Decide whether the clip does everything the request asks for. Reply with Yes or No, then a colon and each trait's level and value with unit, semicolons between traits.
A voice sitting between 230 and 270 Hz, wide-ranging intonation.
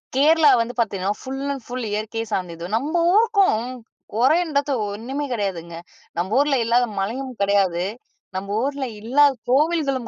Yes: high, 245 Hz; wide, 5.8 semitones